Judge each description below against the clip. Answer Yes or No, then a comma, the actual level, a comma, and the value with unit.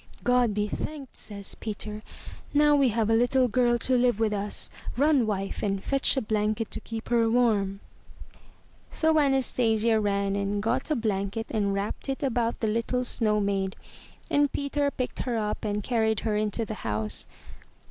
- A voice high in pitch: Yes, high, 225 Hz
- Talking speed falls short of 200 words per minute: Yes, average, 170 wpm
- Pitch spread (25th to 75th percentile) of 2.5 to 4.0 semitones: Yes, average, 3.3 semitones